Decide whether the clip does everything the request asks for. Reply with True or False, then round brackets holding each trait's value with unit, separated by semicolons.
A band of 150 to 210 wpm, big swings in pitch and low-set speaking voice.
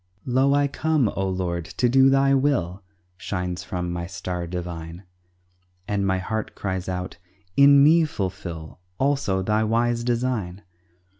False (140 wpm; 6.5 semitones; 100 Hz)